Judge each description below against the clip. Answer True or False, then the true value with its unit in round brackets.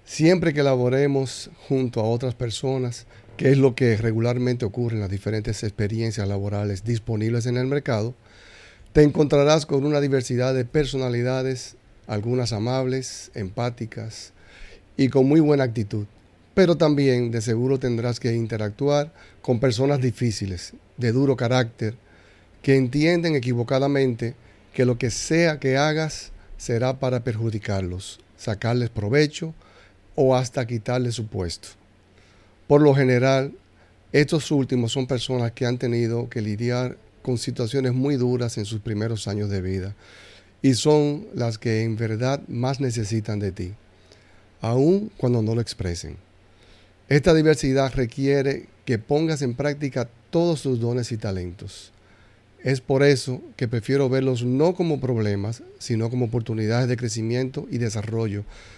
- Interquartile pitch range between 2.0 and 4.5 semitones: True (3.9 semitones)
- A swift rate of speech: False (135 wpm)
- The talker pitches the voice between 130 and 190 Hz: False (120 Hz)